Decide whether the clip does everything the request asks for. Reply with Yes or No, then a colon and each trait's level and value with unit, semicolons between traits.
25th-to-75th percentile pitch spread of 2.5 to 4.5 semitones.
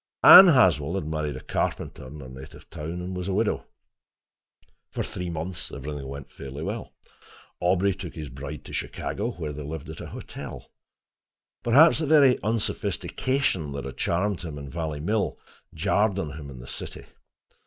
No: average, 5.3 semitones